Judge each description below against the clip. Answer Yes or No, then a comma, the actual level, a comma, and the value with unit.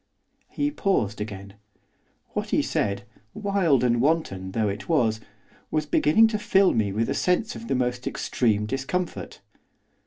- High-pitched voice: No, low, 130 Hz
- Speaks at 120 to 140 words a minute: No, average, 150 wpm